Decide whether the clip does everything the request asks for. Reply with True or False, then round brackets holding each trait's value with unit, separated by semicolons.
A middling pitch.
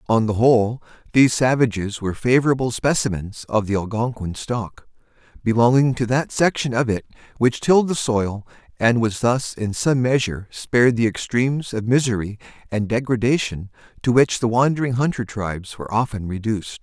False (115 Hz)